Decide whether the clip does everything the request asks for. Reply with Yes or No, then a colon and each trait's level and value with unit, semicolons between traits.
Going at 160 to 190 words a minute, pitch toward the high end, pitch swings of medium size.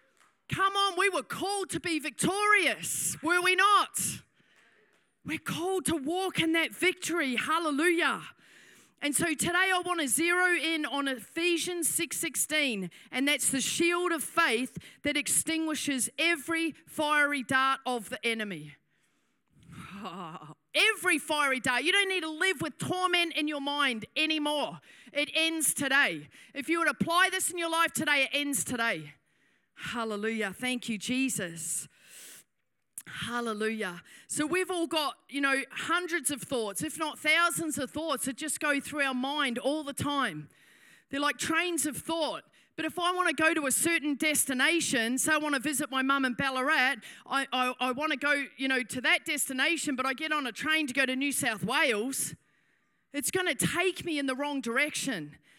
Yes: average, 170 wpm; very high, 290 Hz; average, 4.2 semitones